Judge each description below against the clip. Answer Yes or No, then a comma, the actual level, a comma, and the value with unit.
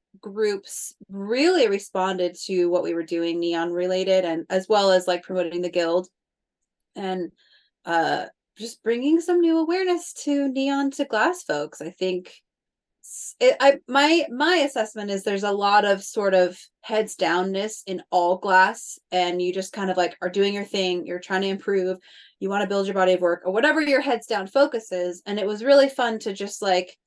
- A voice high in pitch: Yes, high, 200 Hz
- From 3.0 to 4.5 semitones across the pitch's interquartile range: No, average, 5.1 semitones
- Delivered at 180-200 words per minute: Yes, average, 190 wpm